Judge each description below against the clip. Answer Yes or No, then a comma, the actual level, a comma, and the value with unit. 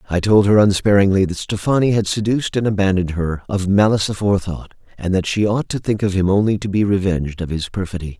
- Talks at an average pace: No, fast, 210 wpm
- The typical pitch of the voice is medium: No, low, 100 Hz